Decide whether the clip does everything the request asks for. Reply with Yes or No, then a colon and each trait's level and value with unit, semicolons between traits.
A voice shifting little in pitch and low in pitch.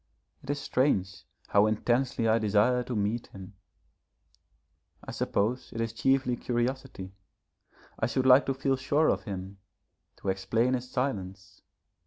No: average, 4.4 semitones; low, 120 Hz